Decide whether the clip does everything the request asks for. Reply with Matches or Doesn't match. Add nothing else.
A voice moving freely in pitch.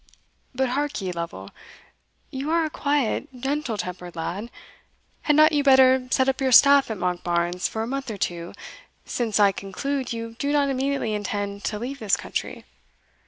Matches